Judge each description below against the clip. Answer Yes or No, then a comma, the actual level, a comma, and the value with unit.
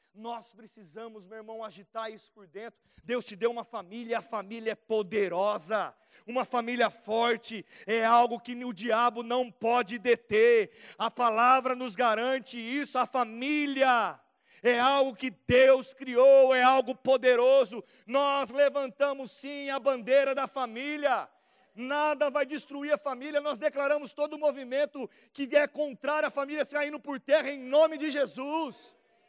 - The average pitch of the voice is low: No, very high, 255 Hz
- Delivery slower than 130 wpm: No, average, 150 wpm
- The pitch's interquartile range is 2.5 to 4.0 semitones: Yes, average, 3.4 semitones